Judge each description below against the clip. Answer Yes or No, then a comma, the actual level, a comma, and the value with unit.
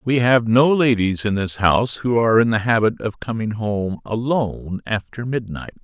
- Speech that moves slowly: No, average, 185 wpm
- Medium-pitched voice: No, low, 115 Hz